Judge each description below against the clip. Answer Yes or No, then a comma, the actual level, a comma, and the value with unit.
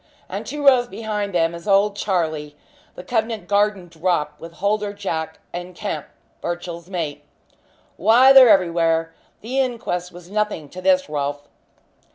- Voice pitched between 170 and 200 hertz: Yes, medium, 185 Hz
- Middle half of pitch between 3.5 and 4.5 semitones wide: Yes, average, 4.1 semitones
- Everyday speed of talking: Yes, average, 145 wpm